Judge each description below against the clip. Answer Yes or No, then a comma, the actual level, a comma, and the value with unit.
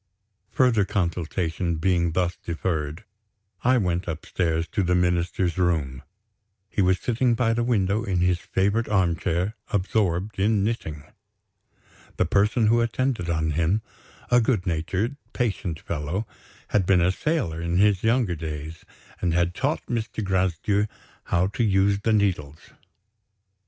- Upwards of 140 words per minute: No, slow, 135 wpm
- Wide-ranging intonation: No, average, 4.1 semitones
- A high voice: No, very low, 95 Hz